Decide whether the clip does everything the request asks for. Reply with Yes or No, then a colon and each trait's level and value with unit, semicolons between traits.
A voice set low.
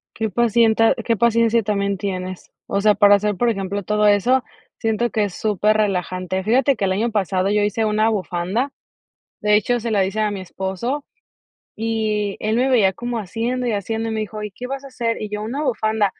No: high, 215 Hz